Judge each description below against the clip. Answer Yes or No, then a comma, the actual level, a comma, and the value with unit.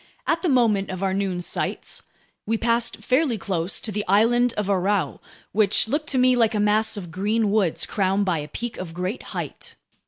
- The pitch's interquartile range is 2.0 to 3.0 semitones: No, average, 3.6 semitones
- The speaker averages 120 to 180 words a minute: No, average, 195 wpm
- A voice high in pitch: Yes, high, 210 Hz